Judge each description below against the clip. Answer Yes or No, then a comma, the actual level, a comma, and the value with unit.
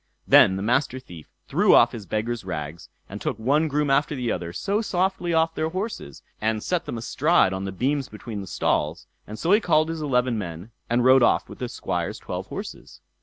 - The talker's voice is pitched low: Yes, low, 125 Hz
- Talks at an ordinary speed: No, fast, 210 wpm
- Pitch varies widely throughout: Yes, wide, 7.9 semitones